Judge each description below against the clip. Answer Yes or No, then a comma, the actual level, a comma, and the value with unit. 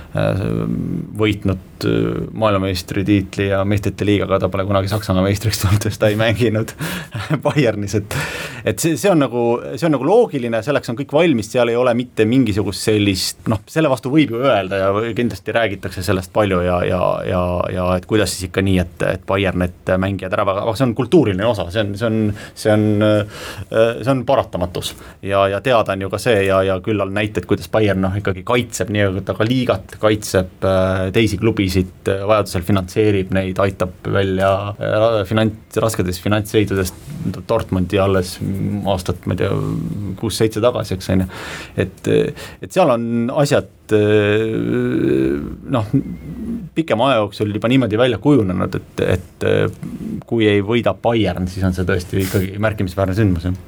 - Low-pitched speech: Yes, low, 105 Hz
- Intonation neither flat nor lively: Yes, average, 3.0 semitones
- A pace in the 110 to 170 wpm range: Yes, average, 160 wpm